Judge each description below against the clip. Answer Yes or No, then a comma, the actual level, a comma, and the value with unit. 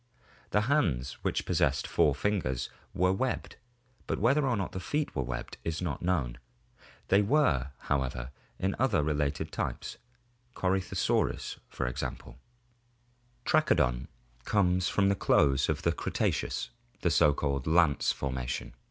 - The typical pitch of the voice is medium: No, very low, 80 Hz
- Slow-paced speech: Yes, slow, 130 wpm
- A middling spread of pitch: No, wide, 6.5 semitones